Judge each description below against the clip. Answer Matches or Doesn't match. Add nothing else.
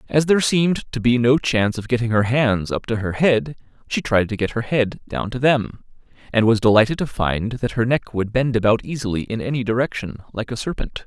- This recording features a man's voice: Matches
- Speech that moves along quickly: Matches